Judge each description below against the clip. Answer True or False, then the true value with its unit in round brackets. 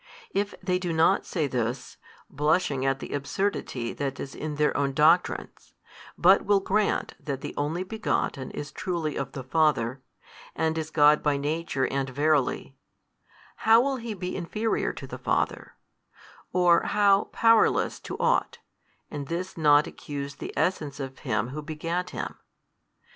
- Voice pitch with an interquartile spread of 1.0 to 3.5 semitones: False (4.5 semitones)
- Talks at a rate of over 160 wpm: False (155 wpm)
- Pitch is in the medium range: True (155 Hz)